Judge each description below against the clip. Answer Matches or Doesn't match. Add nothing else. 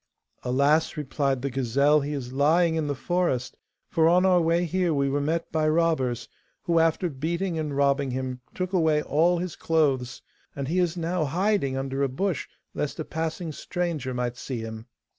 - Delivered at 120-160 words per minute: Doesn't match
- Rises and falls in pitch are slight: Doesn't match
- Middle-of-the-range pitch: Matches